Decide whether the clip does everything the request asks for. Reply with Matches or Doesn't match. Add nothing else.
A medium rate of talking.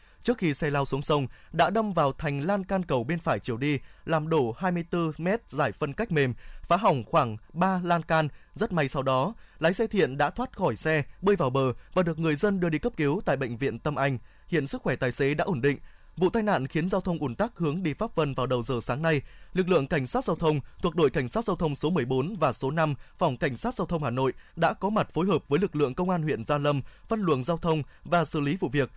Doesn't match